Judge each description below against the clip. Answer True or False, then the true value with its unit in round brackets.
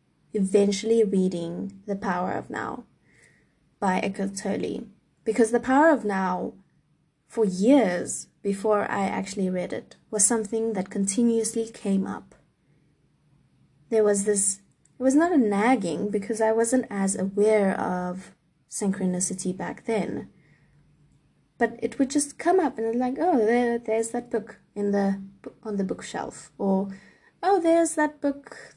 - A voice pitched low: False (210 Hz)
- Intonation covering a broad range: False (3.3 semitones)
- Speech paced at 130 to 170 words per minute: True (140 wpm)